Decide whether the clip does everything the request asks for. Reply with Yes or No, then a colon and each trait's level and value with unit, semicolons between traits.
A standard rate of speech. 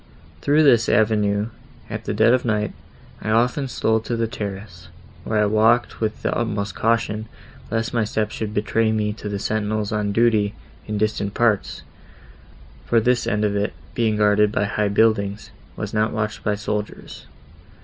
Yes: average, 170 wpm